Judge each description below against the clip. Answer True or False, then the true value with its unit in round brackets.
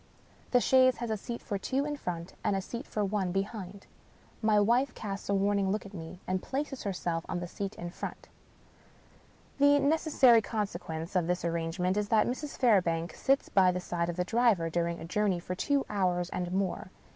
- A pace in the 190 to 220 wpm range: True (200 wpm)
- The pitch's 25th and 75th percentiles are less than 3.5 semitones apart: False (4.8 semitones)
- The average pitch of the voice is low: False (195 Hz)